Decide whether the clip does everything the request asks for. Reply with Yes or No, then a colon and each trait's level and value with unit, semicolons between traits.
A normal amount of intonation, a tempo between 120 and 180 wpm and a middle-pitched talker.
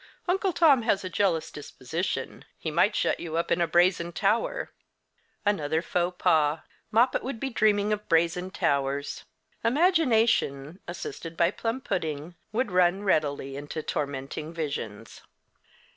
No: wide, 5.9 semitones; slow, 135 wpm; medium, 175 Hz